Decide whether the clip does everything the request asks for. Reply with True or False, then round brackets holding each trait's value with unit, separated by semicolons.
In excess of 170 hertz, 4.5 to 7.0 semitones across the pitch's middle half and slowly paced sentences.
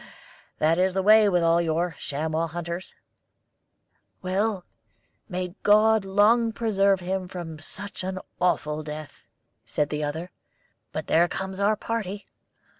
False (185 Hz; 3.7 semitones; 130 wpm)